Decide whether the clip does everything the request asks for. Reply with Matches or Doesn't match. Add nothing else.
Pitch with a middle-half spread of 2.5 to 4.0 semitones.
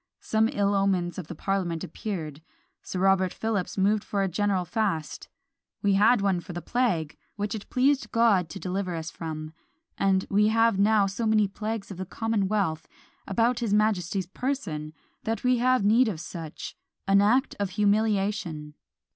Matches